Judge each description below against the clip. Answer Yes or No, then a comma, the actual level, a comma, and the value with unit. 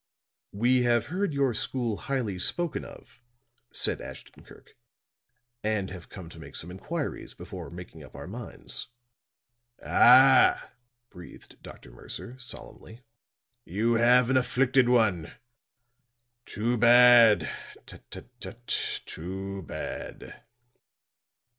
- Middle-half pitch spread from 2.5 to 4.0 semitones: No, average, 4.7 semitones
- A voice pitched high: No, low, 120 Hz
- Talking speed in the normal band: No, slow, 110 wpm